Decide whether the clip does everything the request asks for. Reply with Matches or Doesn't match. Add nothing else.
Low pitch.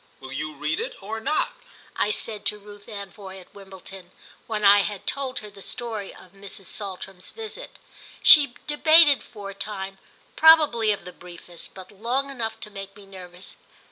Doesn't match